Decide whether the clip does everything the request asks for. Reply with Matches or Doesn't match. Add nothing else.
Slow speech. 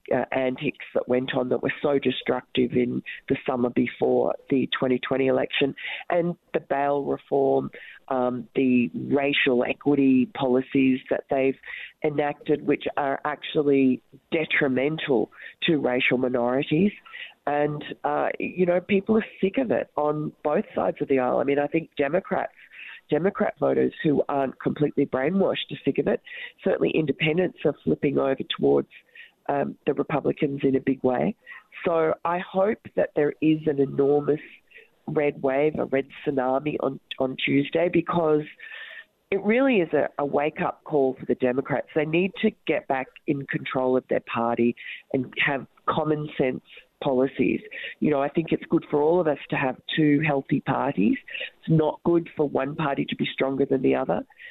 Doesn't match